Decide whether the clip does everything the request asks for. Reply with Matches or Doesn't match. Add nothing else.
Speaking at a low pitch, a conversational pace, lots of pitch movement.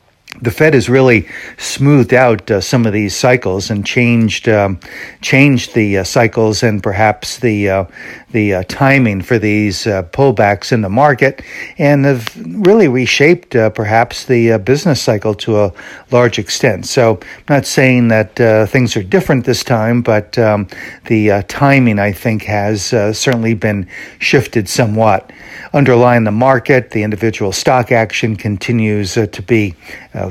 Doesn't match